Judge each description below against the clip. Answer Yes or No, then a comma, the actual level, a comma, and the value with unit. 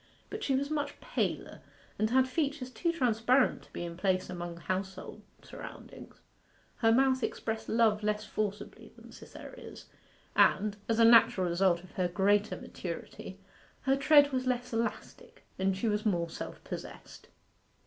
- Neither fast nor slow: Yes, average, 150 wpm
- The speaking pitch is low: No, high, 220 Hz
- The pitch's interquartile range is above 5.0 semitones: Yes, wide, 5.4 semitones